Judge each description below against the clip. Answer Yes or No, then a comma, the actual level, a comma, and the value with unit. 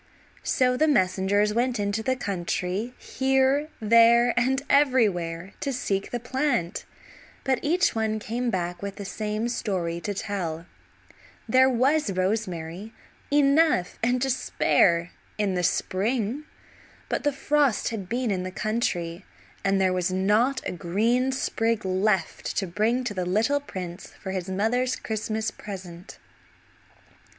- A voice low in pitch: No, high, 215 Hz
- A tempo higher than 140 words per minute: No, slow, 135 wpm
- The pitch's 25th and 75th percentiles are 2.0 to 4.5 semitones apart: No, average, 5.2 semitones